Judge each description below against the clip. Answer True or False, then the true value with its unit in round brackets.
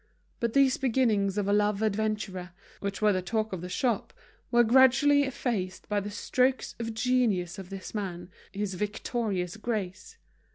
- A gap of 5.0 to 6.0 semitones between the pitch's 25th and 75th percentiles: False (3.7 semitones)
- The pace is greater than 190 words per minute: False (160 wpm)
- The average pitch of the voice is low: False (210 Hz)